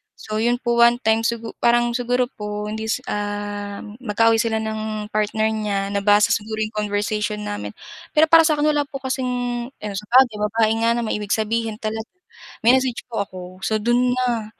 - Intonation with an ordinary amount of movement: No, narrow, 2.3 semitones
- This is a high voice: Yes, high, 220 Hz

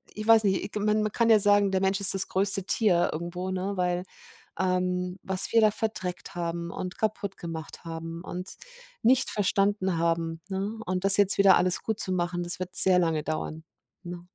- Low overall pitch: No, medium, 185 Hz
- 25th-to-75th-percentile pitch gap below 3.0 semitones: Yes, narrow, 2.5 semitones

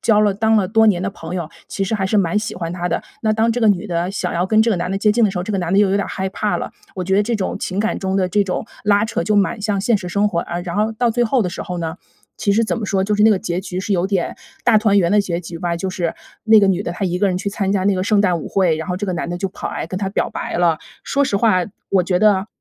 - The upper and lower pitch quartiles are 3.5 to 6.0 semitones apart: No, average, 2.8 semitones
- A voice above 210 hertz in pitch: No, high, 195 Hz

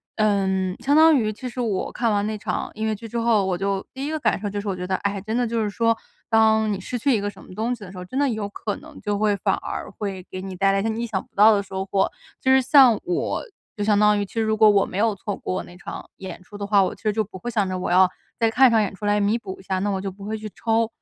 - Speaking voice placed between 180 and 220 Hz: Yes, high, 210 Hz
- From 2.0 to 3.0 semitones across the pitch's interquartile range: Yes, narrow, 2.5 semitones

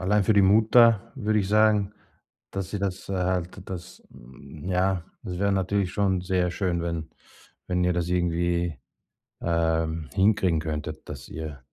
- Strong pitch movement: No, average, 2.7 semitones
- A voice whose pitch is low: Yes, very low, 90 Hz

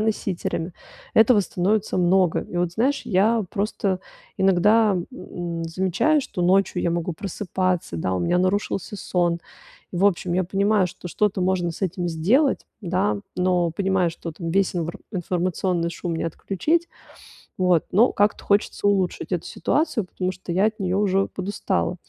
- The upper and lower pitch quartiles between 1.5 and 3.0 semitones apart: Yes, narrow, 2.6 semitones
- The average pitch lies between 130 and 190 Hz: Yes, medium, 185 Hz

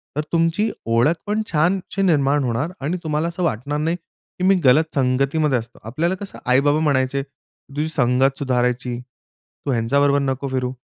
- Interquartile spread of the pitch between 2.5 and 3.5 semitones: No, average, 4.1 semitones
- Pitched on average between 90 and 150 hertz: Yes, medium, 140 Hz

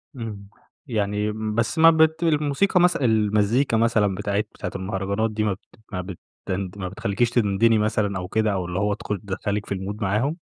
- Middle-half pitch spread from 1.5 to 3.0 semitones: Yes, narrow, 2.6 semitones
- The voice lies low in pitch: Yes, low, 105 Hz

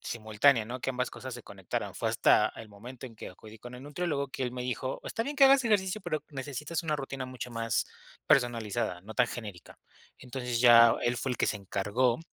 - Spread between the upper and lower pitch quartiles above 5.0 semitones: No, average, 3.3 semitones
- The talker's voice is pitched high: No, low, 125 Hz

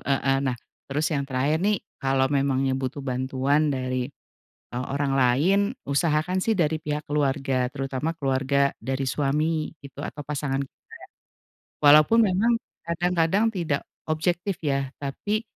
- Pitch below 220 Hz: Yes, medium, 140 Hz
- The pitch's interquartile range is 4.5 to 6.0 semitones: No, average, 2.9 semitones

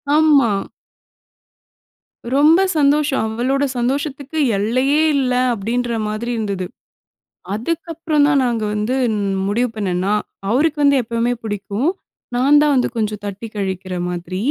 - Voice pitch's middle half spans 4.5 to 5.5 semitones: Yes, average, 5.2 semitones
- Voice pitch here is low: No, high, 245 Hz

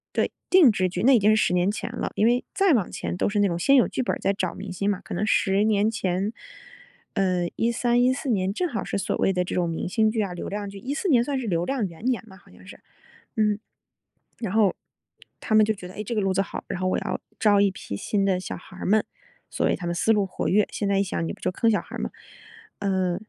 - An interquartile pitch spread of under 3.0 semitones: No, average, 3.3 semitones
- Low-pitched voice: No, high, 205 Hz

